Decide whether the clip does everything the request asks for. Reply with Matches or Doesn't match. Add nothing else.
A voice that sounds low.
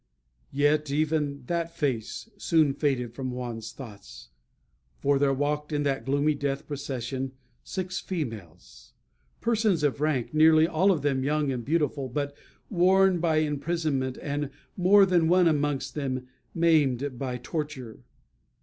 Doesn't match